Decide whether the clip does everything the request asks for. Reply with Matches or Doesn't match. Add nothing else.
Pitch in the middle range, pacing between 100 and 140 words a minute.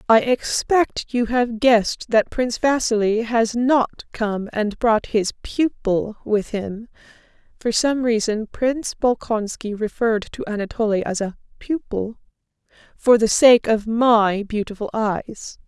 Doesn't match